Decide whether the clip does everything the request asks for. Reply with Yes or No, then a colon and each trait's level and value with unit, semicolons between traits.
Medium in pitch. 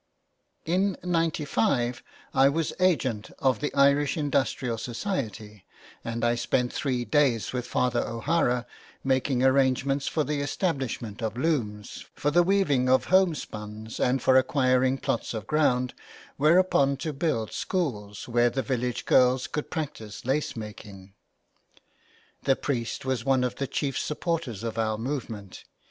No: low, 130 Hz